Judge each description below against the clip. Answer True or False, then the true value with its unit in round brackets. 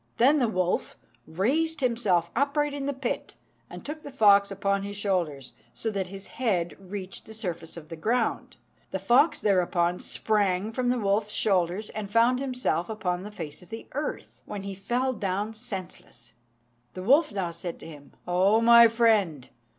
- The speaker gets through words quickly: False (175 wpm)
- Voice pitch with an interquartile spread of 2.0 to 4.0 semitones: False (4.7 semitones)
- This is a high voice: True (205 Hz)